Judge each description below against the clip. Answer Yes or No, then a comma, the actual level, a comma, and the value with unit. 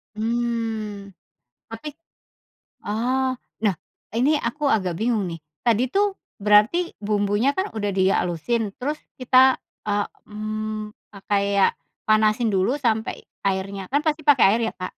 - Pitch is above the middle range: Yes, high, 220 Hz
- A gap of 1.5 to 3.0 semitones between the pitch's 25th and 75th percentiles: No, average, 3.4 semitones